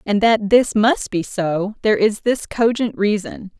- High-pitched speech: Yes, high, 210 Hz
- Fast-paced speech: No, average, 185 wpm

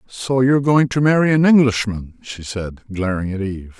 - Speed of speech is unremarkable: Yes, average, 190 wpm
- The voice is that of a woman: No, male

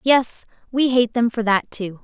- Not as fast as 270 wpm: Yes, fast, 205 wpm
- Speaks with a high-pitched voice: Yes, high, 235 Hz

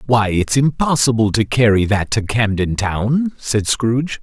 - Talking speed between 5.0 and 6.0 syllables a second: No, 4.2 syllables/s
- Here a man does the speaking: Yes, male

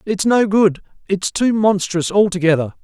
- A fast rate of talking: No, average, 150 wpm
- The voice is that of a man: Yes, male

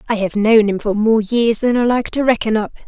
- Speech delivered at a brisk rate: Yes, fast, 270 wpm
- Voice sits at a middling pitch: No, high, 220 Hz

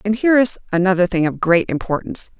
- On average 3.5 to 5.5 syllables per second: No, 6.6 syllables/s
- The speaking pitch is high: Yes, high, 195 Hz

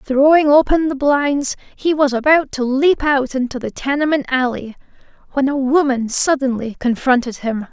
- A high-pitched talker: Yes, very high, 270 Hz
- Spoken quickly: No, average, 155 wpm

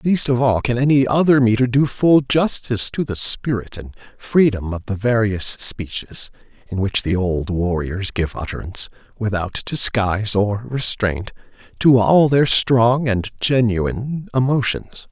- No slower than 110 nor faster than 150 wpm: Yes, average, 145 wpm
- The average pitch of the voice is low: Yes, low, 115 Hz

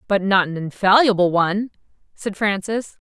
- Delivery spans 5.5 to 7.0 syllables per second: No, 5.0 syllables/s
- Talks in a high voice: Yes, high, 200 Hz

